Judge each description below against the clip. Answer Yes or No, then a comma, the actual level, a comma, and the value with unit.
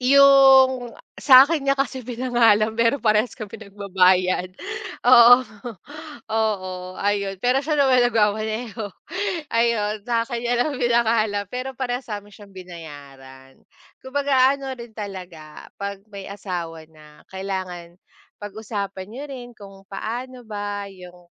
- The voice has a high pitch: Yes, high, 215 Hz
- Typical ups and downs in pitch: Yes, average, 4.5 semitones